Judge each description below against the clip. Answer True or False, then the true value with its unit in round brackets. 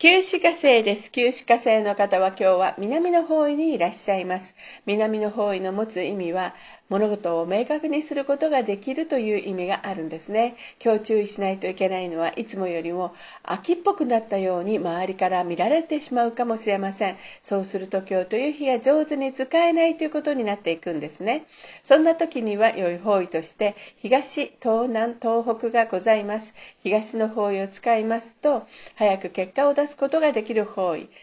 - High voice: True (215 Hz)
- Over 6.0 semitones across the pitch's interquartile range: False (5.7 semitones)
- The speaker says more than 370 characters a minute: True (380 characters per minute)